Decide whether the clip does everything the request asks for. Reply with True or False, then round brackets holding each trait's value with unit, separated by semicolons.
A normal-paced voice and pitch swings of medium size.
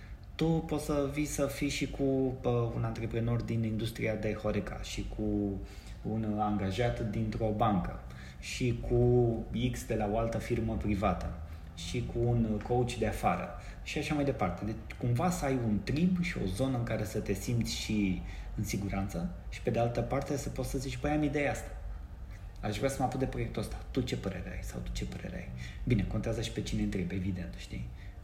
False (200 wpm; 4.0 semitones)